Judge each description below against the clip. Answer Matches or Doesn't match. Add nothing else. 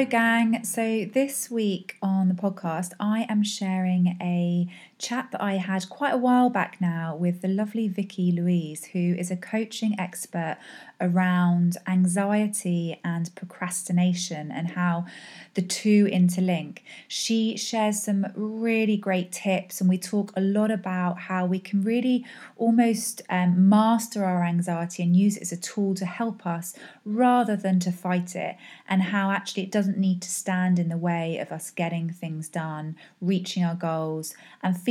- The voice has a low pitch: Doesn't match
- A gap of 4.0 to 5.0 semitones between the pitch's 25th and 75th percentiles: Doesn't match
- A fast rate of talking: Doesn't match